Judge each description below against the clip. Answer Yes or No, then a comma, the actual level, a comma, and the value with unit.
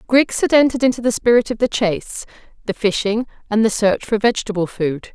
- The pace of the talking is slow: No, average, 200 wpm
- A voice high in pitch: Yes, high, 220 Hz